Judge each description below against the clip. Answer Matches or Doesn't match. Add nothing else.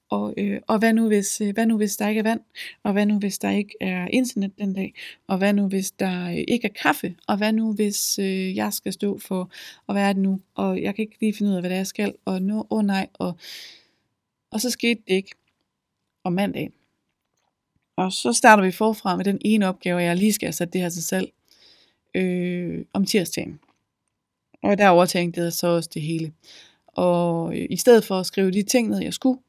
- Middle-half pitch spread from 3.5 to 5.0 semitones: Doesn't match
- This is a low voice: Doesn't match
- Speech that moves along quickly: Matches